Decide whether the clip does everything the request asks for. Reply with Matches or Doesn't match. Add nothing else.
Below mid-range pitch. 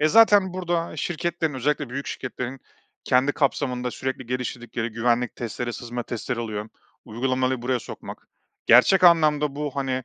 Matches